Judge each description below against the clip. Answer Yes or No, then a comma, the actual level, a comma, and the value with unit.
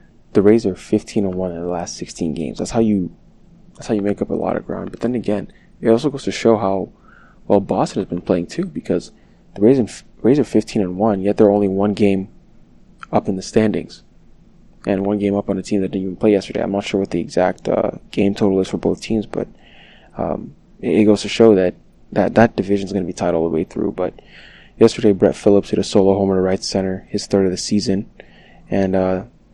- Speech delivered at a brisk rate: Yes, fast, 240 wpm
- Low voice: Yes, low, 100 Hz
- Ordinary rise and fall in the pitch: No, narrow, 2.2 semitones